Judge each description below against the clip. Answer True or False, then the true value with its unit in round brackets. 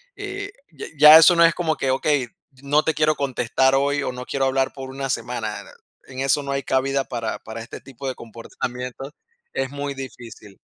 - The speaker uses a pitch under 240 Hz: True (135 Hz)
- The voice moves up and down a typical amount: False (2.3 semitones)